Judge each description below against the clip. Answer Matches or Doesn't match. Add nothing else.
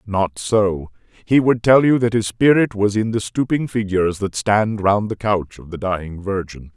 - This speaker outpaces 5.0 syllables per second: Doesn't match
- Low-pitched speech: Matches